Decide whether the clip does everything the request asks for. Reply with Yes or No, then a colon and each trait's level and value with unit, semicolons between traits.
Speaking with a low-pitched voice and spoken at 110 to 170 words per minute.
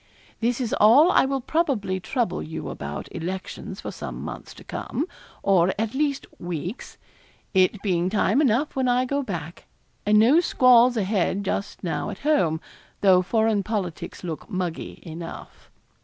No: high, 210 Hz; average, 155 wpm